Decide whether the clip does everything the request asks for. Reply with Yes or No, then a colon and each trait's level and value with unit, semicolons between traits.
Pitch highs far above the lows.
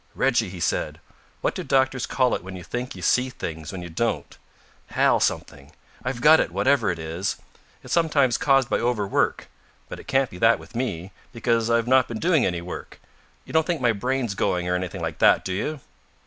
Yes: wide, 6.3 semitones